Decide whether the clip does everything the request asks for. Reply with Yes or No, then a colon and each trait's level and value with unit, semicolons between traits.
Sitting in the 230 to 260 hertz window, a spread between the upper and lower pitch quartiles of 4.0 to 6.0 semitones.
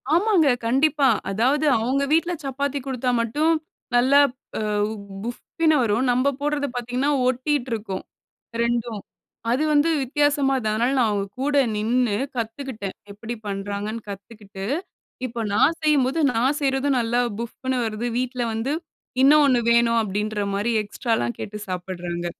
Yes: high, 245 Hz; average, 4.5 semitones